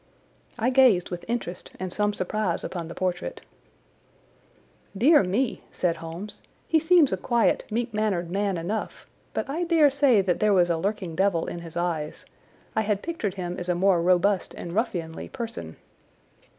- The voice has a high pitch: Yes, high, 195 Hz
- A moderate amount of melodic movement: Yes, average, 4.7 semitones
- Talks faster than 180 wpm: No, average, 165 wpm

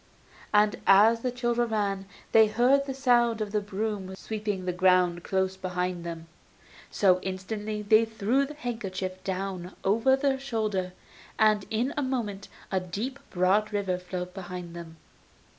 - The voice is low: No, high, 205 Hz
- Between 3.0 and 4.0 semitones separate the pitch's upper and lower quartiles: Yes, average, 3.6 semitones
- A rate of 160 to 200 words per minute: No, average, 150 wpm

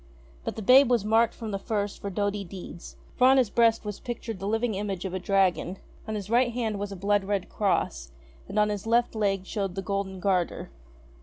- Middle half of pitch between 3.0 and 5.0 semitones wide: No, narrow, 2.5 semitones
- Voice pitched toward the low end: No, high, 205 Hz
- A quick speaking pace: Yes, fast, 220 wpm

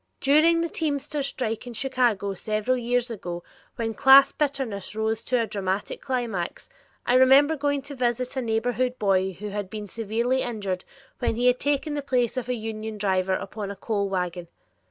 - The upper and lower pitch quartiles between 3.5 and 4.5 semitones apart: Yes, average, 4.2 semitones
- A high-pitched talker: Yes, high, 235 Hz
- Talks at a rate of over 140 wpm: Yes, average, 175 wpm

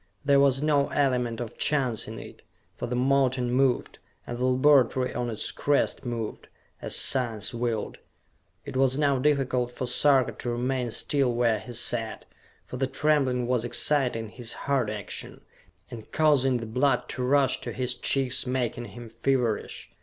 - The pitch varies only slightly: Yes, narrow, 2.2 semitones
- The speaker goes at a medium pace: Yes, average, 160 wpm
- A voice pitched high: No, low, 125 Hz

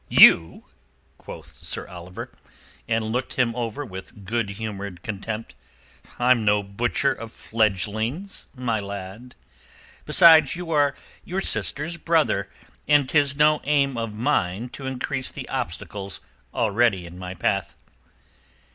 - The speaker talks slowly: Yes, slow, 125 wpm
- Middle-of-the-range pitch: No, low, 115 Hz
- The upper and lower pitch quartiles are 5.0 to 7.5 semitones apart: Yes, wide, 5.6 semitones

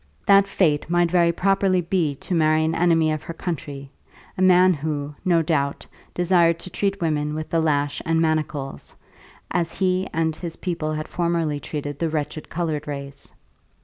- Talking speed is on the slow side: No, average, 170 wpm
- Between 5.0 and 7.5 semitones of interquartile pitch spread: No, narrow, 2.6 semitones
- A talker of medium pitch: Yes, medium, 165 Hz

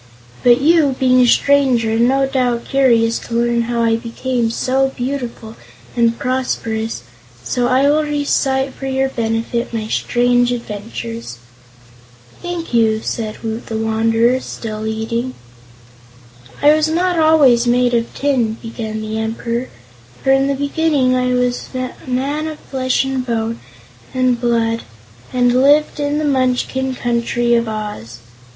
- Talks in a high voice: Yes, high, 245 Hz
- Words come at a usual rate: Yes, average, 145 wpm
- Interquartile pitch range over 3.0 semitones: No, average, 2.7 semitones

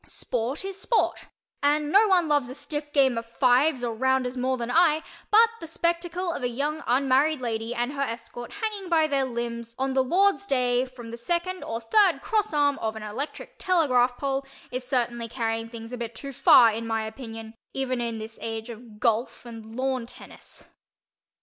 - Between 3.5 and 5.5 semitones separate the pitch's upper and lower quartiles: Yes, average, 4.5 semitones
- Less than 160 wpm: No, average, 190 wpm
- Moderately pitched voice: No, very high, 255 Hz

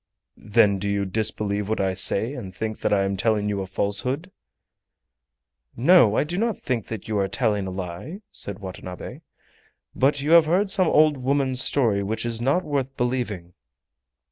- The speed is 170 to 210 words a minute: Yes, average, 175 wpm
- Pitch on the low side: Yes, low, 110 Hz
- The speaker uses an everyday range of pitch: No, wide, 5.8 semitones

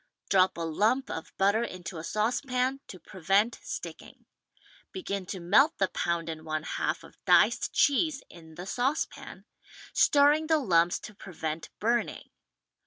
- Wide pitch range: Yes, wide, 7.2 semitones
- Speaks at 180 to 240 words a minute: No, average, 145 wpm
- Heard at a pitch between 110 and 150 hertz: No, high, 195 Hz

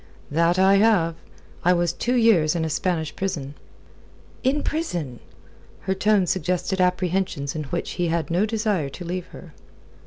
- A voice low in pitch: No, medium, 180 Hz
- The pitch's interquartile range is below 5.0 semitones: Yes, average, 2.9 semitones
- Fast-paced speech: No, average, 155 wpm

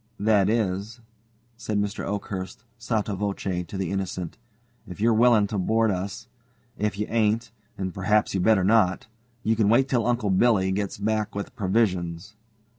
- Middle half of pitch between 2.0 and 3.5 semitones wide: Yes, narrow, 2.6 semitones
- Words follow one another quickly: No, average, 160 wpm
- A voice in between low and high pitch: No, low, 105 Hz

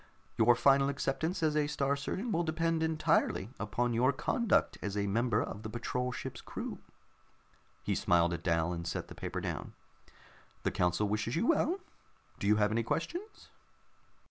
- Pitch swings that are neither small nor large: No, wide, 7.3 semitones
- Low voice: Yes, low, 125 Hz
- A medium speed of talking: Yes, average, 170 wpm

